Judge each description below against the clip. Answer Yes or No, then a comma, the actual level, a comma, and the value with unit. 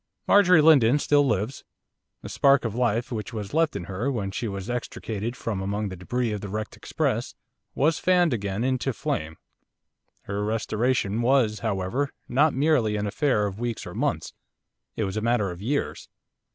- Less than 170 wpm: No, average, 175 wpm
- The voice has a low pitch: Yes, low, 115 Hz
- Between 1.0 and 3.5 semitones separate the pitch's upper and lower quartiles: No, average, 4.7 semitones